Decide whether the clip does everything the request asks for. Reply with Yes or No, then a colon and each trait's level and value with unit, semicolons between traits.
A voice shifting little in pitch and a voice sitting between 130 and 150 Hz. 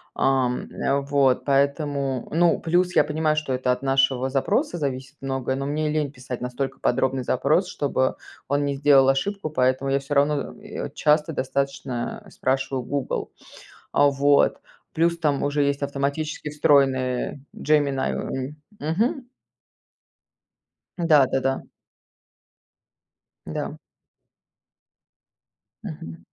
Yes: narrow, 2.1 semitones; medium, 140 Hz